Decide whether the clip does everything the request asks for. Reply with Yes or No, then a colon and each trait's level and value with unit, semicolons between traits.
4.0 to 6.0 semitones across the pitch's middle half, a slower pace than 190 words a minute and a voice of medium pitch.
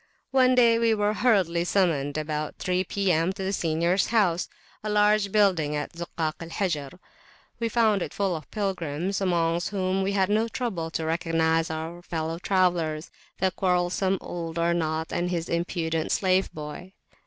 No: average, 3.3 semitones; average, 165 wpm; medium, 175 Hz